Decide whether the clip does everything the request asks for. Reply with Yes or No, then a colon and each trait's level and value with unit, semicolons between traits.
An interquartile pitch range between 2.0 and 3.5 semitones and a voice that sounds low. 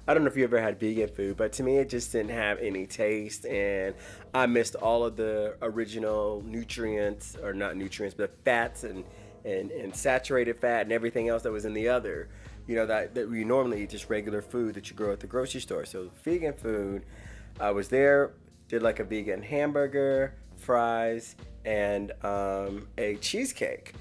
Yes: average, 2.8 semitones; low, 110 Hz